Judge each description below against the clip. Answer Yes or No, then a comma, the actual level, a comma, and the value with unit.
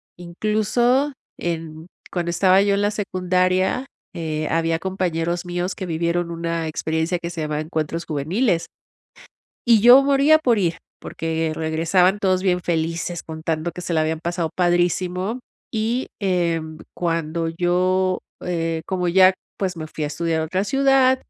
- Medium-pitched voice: Yes, medium, 175 Hz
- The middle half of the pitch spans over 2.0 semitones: Yes, narrow, 2.5 semitones